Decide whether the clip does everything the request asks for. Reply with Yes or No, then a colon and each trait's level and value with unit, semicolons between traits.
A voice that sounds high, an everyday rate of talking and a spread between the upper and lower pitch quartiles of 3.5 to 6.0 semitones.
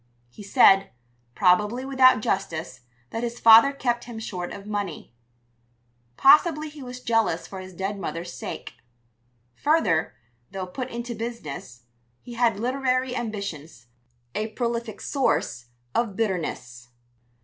No: high, 220 Hz; slow, 125 wpm; average, 5.2 semitones